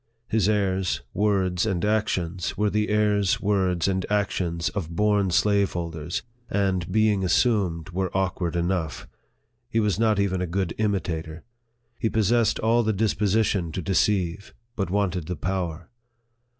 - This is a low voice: Yes, very low, 95 Hz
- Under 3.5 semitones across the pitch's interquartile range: Yes, average, 3.0 semitones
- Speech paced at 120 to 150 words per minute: Yes, slow, 135 wpm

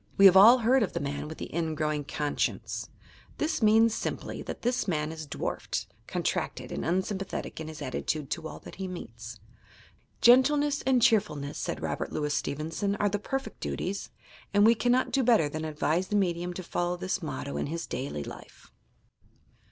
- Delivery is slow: No, average, 180 wpm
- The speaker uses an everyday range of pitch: No, wide, 6.3 semitones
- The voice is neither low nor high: Yes, medium, 180 Hz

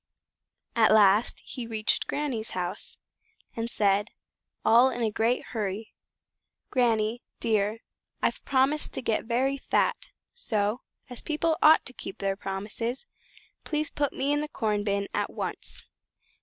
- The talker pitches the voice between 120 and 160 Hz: No, high, 230 Hz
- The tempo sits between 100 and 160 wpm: Yes, average, 145 wpm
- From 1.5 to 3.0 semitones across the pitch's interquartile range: No, average, 4.1 semitones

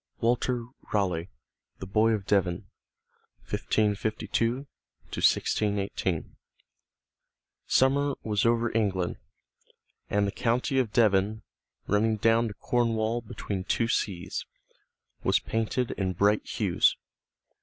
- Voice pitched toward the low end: Yes, low, 110 Hz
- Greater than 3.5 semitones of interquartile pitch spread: No, average, 2.7 semitones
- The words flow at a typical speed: No, slow, 100 wpm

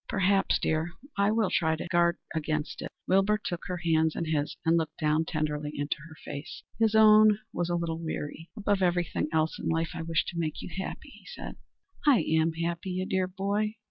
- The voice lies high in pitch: No, medium, 170 Hz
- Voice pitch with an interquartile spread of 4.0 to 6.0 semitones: No, average, 3.3 semitones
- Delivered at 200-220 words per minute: Yes, fast, 205 wpm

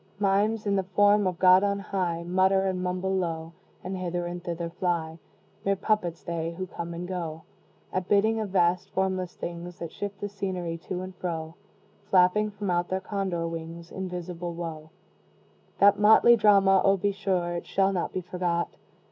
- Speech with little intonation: Yes, narrow, 2.3 semitones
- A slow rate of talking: No, average, 175 wpm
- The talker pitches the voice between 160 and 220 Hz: Yes, medium, 185 Hz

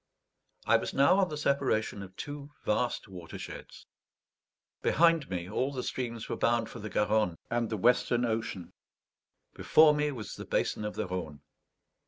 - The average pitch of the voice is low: Yes, low, 115 Hz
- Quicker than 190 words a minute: No, average, 160 wpm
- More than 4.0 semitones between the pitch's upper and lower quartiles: Yes, average, 5.1 semitones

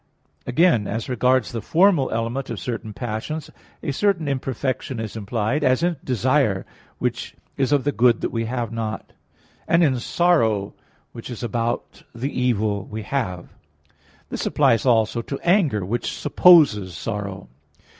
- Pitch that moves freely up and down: No, average, 4.1 semitones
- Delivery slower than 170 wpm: Yes, average, 145 wpm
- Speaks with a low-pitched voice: Yes, low, 120 Hz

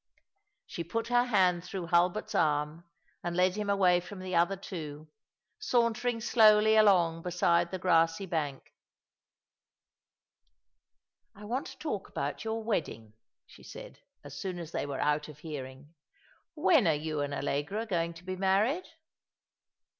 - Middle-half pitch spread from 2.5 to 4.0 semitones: No, average, 5.0 semitones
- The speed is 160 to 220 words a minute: No, average, 145 wpm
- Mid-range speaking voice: Yes, medium, 180 Hz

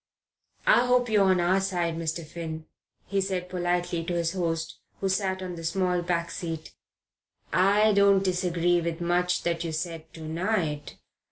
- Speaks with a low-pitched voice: No, medium, 175 Hz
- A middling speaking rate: Yes, average, 165 wpm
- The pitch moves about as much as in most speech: No, narrow, 2.3 semitones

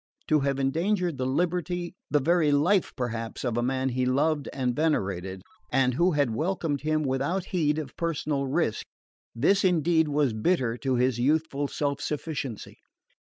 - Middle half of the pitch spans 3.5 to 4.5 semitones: Yes, average, 4.0 semitones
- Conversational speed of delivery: Yes, average, 160 wpm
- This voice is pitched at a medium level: Yes, medium, 145 Hz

